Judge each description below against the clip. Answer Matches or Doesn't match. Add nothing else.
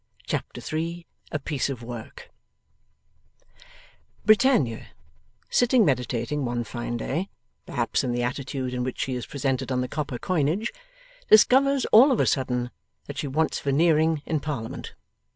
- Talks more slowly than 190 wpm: Matches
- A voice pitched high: Doesn't match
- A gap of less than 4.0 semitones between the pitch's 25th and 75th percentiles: Doesn't match